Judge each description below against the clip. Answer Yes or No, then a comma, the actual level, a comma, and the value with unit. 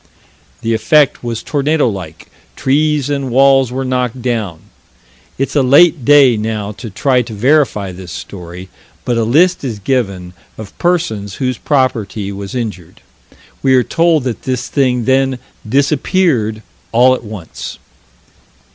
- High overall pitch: No, low, 125 Hz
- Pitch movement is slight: No, average, 4.4 semitones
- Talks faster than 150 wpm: No, average, 140 wpm